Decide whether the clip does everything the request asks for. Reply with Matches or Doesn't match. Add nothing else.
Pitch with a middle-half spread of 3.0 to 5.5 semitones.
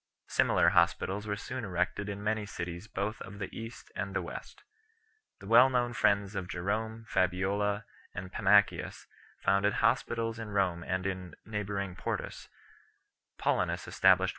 Doesn't match